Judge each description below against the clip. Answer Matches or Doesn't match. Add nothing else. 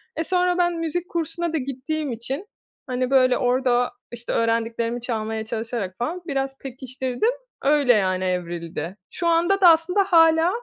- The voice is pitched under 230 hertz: Doesn't match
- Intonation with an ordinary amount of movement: Doesn't match